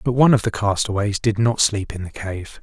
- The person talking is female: No, male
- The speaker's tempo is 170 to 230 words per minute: No, fast, 250 wpm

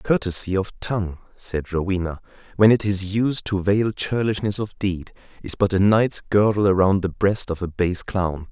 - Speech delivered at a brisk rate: No, average, 185 wpm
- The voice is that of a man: Yes, male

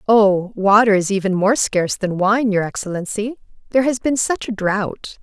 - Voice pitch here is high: Yes, high, 210 Hz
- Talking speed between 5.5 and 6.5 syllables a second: No, 4.9 syllables/s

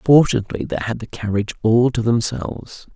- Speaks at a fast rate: No, average, 165 wpm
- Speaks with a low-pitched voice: Yes, low, 115 Hz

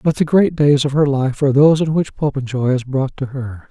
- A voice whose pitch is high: No, medium, 140 Hz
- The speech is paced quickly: Yes, fast, 260 wpm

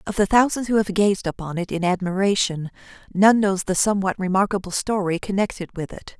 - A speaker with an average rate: Yes, average, 185 wpm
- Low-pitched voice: No, high, 195 Hz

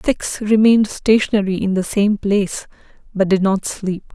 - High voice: Yes, high, 200 Hz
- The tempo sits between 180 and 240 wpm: No, average, 160 wpm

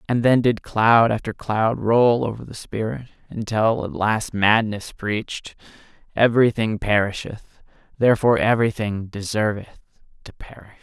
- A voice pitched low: Yes, low, 110 Hz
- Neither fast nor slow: No, slow, 120 wpm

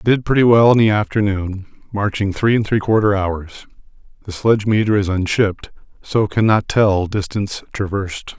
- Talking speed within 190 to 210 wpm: No, average, 155 wpm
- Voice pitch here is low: Yes, low, 105 Hz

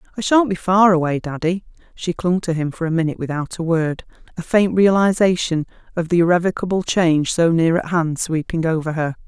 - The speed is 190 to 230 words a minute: Yes, average, 195 wpm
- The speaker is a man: No, female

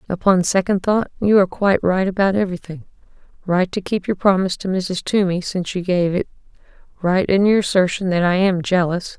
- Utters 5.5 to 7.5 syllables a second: Yes, 5.8 syllables/s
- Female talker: Yes, female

